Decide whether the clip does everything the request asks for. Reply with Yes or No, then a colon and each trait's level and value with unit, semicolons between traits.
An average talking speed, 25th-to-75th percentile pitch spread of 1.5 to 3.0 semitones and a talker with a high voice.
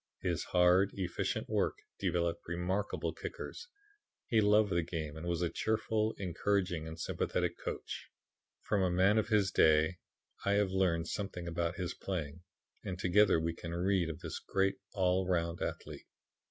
No: average, 155 wpm; narrow, 2.6 semitones; very low, 90 Hz